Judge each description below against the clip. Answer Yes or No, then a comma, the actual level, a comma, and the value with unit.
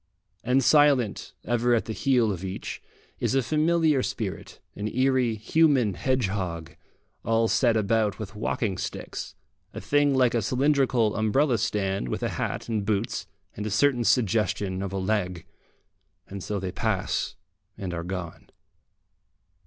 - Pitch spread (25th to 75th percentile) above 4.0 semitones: Yes, average, 4.8 semitones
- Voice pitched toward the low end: Yes, low, 110 Hz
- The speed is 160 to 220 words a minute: No, average, 145 wpm